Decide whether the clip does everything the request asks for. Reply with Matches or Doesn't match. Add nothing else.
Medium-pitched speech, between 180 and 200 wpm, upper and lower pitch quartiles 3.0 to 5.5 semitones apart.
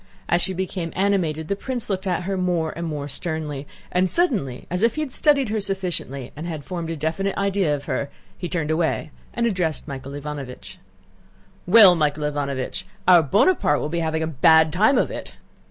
Matches